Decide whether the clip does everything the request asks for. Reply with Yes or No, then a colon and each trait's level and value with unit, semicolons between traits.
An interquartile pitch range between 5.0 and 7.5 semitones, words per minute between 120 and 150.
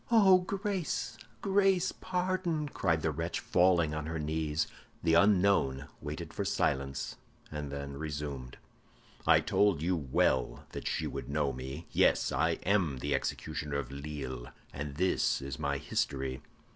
Yes: wide, 5.4 semitones; average, 145 wpm